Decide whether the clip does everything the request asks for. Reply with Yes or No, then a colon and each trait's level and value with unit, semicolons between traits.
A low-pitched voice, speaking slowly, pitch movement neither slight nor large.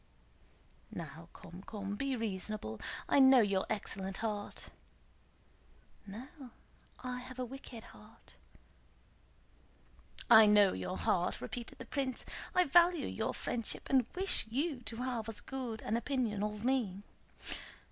No: high, 230 Hz; slow, 125 wpm; average, 4.1 semitones